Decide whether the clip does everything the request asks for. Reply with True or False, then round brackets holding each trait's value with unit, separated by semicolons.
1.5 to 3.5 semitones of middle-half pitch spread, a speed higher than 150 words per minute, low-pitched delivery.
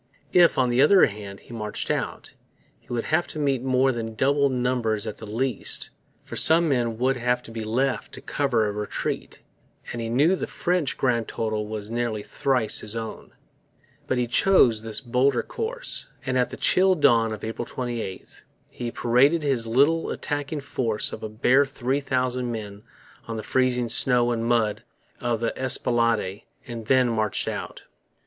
True (3.0 semitones; 175 wpm; 120 Hz)